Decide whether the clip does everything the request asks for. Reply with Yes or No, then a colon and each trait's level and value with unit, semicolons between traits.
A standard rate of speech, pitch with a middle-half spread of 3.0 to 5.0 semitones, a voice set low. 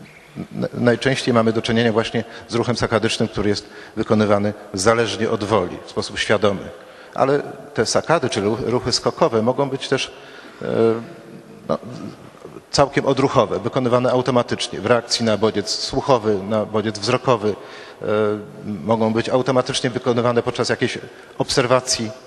No: average, 130 wpm; narrow, 2.4 semitones; low, 115 Hz